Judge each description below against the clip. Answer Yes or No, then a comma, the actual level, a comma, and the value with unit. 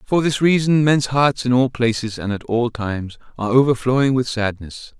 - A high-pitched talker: No, low, 125 Hz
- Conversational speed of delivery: Yes, average, 190 wpm